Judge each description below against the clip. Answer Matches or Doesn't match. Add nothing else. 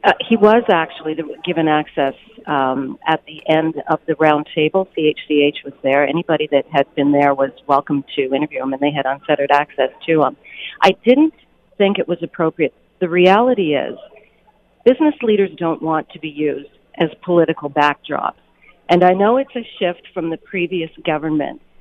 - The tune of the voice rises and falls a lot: Doesn't match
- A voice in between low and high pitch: Matches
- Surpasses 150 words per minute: Matches